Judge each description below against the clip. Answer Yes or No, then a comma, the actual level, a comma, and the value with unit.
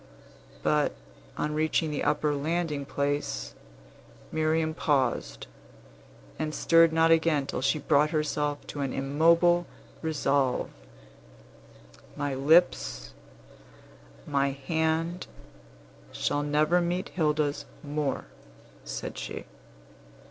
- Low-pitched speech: No, medium, 150 Hz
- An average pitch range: No, narrow, 2.2 semitones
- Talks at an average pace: No, slow, 100 wpm